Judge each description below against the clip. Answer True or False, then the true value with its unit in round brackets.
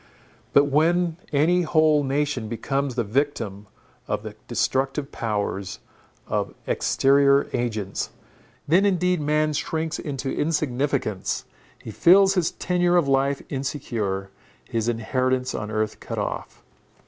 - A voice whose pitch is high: False (140 Hz)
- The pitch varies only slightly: False (5.0 semitones)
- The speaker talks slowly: True (120 wpm)